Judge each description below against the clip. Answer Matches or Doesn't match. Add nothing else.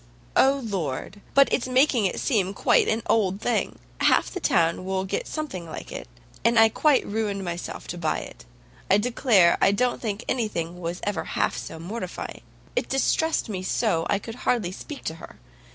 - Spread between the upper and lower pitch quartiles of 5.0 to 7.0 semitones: Matches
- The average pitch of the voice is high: Matches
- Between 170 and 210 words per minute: Matches